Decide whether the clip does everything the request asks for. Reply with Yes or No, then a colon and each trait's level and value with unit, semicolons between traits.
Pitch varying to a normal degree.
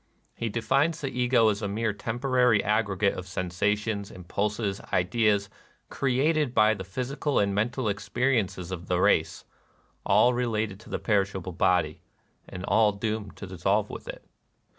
Yes: average, 3.7 semitones